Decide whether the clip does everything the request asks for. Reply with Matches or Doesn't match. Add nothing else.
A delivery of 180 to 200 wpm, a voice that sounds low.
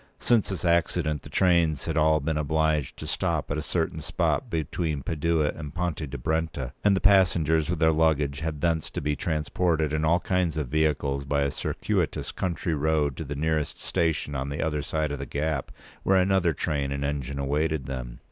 Matches